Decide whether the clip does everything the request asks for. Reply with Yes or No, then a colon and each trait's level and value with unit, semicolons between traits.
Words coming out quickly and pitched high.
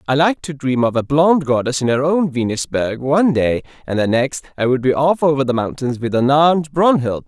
No: fast, 230 wpm; medium, 140 Hz